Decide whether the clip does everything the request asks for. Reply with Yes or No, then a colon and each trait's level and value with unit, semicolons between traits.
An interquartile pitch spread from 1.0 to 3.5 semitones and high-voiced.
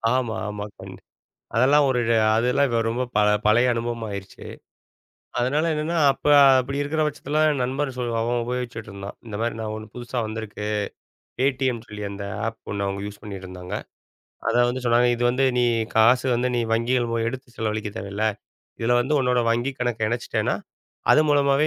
No: average, 3.1 semitones; low, 120 Hz